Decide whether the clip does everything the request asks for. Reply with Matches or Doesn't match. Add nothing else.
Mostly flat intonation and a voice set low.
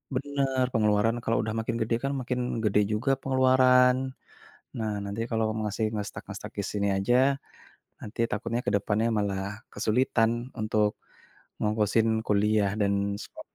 Doesn't match